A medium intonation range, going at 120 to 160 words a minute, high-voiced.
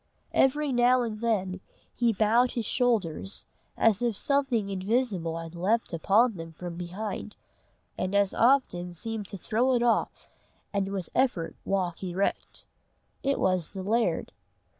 Yes: average, 4.6 semitones; average, 140 wpm; high, 205 Hz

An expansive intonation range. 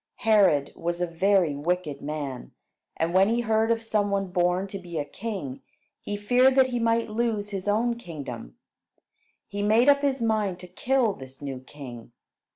Yes: wide, 6.4 semitones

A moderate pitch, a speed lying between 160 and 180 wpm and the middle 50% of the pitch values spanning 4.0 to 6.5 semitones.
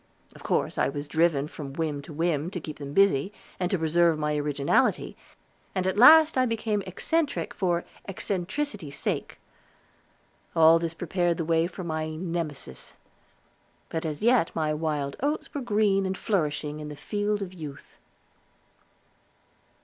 No: medium, 165 Hz; average, 150 wpm; average, 4.5 semitones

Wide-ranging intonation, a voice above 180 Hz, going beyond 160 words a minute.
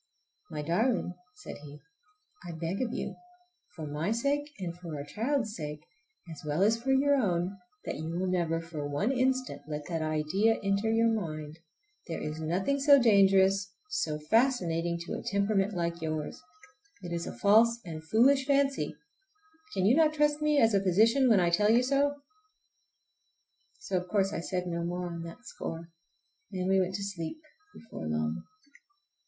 Yes: wide, 5.7 semitones; high, 190 Hz; average, 170 wpm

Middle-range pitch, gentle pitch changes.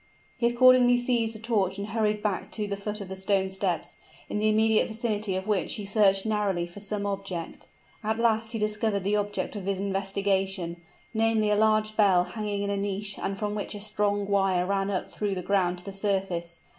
No: high, 205 Hz; narrow, 1.8 semitones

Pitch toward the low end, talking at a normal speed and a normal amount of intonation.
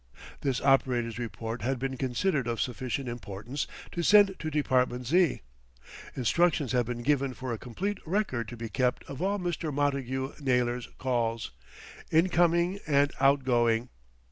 Yes: low, 130 Hz; average, 150 wpm; average, 4.0 semitones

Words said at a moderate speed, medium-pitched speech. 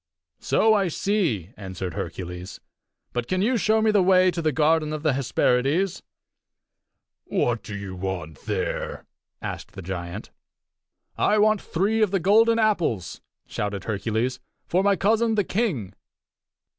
Yes: average, 145 wpm; medium, 155 Hz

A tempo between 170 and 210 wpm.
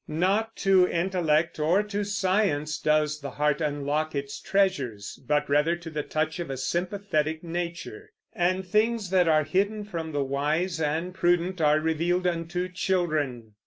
No: average, 155 wpm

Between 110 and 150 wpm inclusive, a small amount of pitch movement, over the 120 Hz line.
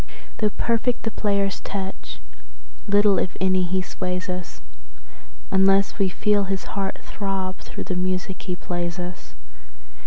Yes: slow, 135 wpm; narrow, 1.6 semitones; high, 190 Hz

